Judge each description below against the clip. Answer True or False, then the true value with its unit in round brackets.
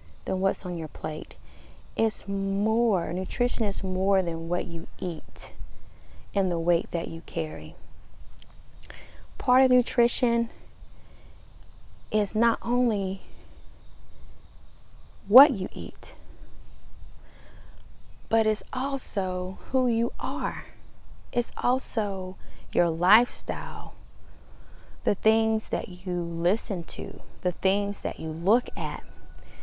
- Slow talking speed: True (105 wpm)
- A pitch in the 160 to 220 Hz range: True (185 Hz)